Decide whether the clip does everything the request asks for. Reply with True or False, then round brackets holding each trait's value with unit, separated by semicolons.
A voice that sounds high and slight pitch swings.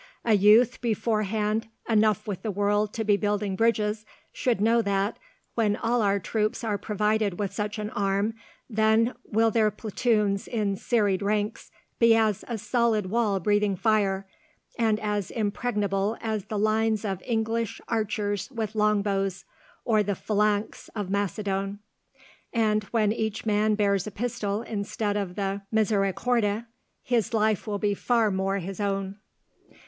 True (210 Hz; 1.6 semitones)